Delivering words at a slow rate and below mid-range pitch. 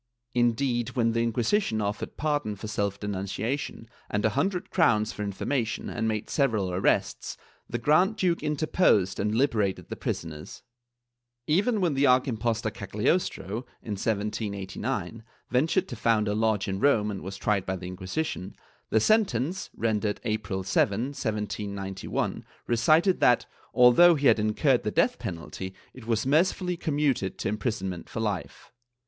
No: average, 150 wpm; low, 110 Hz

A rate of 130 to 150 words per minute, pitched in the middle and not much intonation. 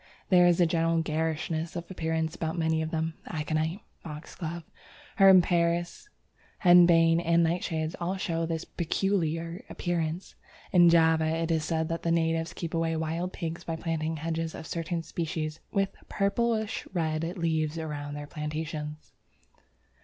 Yes: average, 145 wpm; medium, 165 Hz; narrow, 1.3 semitones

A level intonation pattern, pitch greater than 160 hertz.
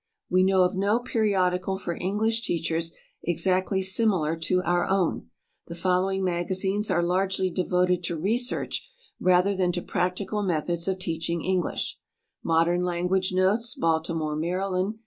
Yes: narrow, 1.9 semitones; medium, 185 Hz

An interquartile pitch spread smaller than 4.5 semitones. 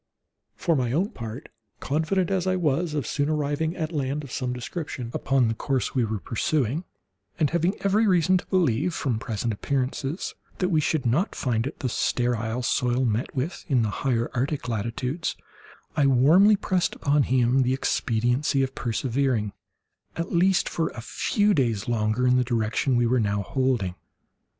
No: average, 5.0 semitones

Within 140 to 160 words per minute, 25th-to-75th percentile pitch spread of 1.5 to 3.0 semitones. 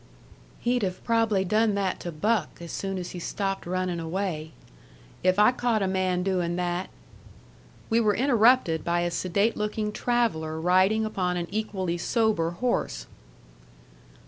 No: average, 150 wpm; average, 3.8 semitones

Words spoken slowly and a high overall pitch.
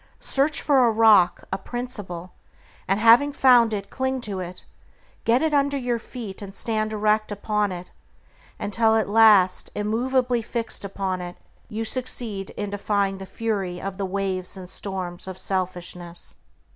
No: average, 155 wpm; high, 210 Hz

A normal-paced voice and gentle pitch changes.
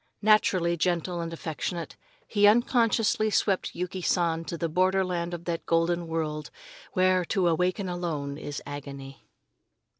No: slow, 130 wpm; narrow, 2.3 semitones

